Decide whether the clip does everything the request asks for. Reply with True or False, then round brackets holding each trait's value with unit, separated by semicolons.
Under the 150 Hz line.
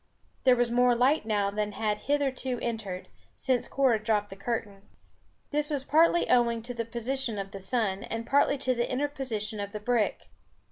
False (235 Hz)